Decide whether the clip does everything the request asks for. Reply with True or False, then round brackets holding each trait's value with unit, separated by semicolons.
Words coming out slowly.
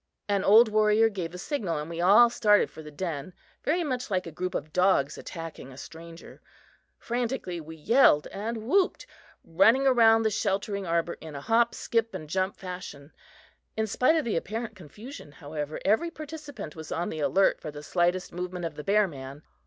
False (185 wpm)